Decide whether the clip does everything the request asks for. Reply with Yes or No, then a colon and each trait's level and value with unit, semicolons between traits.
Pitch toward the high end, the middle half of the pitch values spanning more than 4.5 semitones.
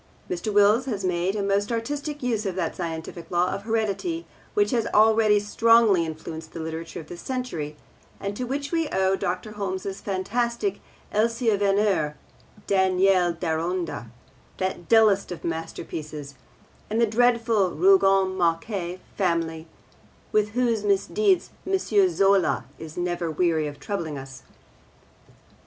Yes: high, 195 Hz; average, 4.9 semitones